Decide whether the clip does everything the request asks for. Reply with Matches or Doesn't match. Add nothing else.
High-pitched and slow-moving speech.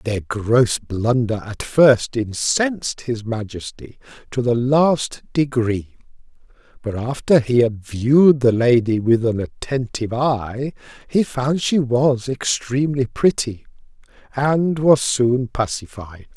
Doesn't match